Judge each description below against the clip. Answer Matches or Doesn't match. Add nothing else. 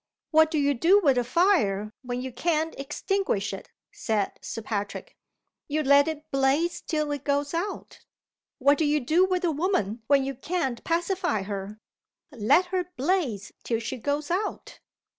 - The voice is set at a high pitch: Matches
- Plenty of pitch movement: Matches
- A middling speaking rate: Matches